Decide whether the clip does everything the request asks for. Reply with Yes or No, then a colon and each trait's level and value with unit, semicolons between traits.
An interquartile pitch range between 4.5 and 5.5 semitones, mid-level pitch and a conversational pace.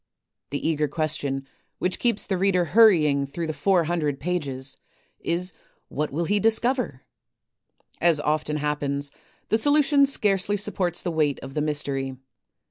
Yes: average, 5.2 semitones; medium, 160 Hz; average, 150 wpm